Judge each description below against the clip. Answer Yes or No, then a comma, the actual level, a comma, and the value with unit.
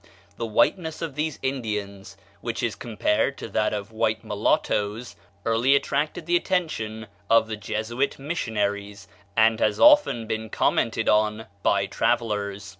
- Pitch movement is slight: No, average, 4.2 semitones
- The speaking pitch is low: Yes, low, 110 Hz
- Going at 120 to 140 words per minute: Yes, slow, 135 wpm